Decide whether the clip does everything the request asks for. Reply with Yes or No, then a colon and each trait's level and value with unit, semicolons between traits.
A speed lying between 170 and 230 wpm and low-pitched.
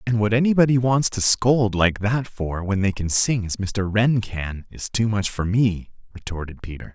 Yes: fast, 205 wpm; low, 105 Hz